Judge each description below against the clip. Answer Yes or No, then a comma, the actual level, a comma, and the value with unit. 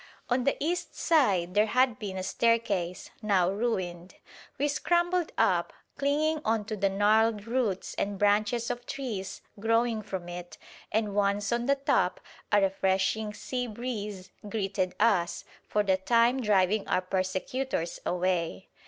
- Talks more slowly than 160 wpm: Yes, average, 145 wpm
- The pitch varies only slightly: No, average, 4.1 semitones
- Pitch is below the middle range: No, high, 210 Hz